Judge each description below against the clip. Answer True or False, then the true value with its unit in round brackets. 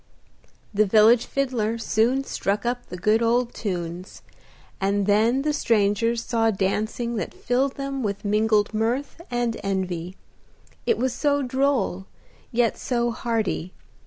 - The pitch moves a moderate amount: True (3.3 semitones)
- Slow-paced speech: True (130 wpm)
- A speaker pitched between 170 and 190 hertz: False (225 Hz)